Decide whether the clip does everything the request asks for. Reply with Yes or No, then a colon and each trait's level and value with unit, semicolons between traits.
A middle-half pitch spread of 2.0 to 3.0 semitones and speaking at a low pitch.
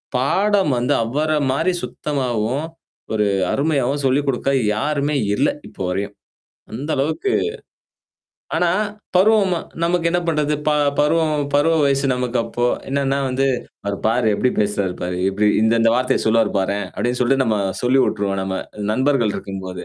No: average, 5.2 semitones; low, 130 Hz